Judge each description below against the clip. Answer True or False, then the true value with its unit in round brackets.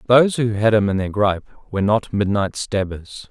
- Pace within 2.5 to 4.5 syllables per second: False (5.1 syllables/s)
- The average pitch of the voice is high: False (105 Hz)